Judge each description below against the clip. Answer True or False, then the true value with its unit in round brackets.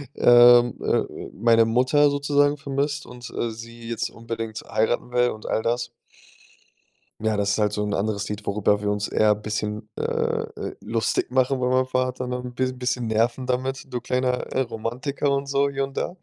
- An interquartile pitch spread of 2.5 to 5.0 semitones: True (2.8 semitones)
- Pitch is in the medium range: False (120 Hz)